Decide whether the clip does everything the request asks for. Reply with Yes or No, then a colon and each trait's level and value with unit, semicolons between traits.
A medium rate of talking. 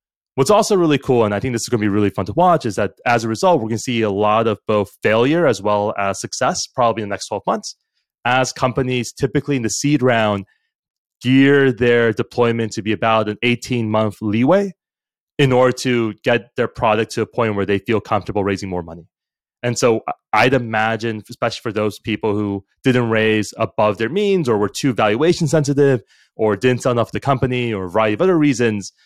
No: fast, 215 wpm